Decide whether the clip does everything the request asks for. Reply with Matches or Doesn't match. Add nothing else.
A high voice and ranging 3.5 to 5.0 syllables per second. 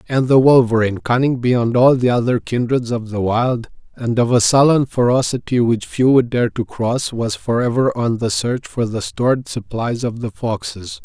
Doesn't match